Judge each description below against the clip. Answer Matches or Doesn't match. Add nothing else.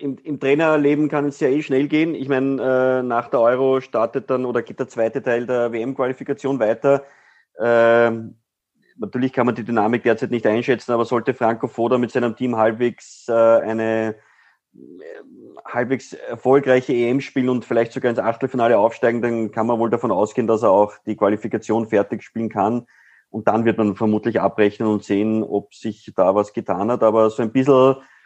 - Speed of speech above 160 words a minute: Matches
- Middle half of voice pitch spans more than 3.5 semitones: Doesn't match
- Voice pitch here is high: Doesn't match